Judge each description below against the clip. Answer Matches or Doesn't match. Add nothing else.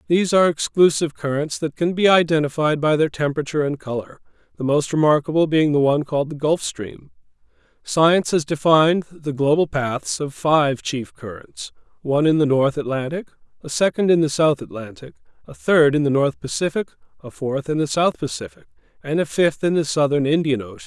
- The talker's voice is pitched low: Doesn't match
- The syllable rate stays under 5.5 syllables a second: Doesn't match